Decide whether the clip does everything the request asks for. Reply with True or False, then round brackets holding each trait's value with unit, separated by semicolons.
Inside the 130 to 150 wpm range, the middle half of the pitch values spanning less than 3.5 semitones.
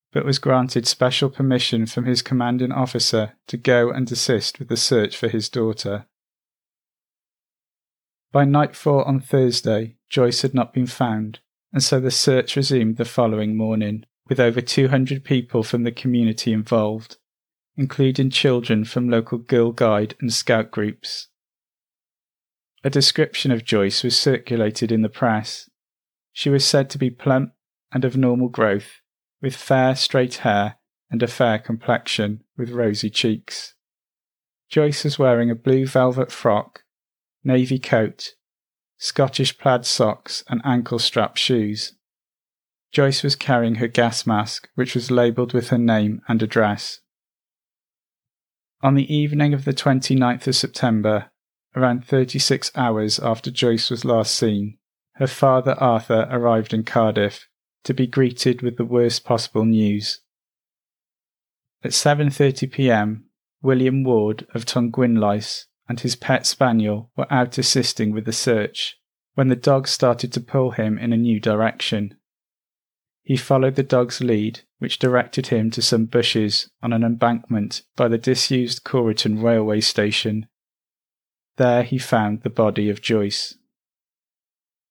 True (140 wpm; 2.8 semitones)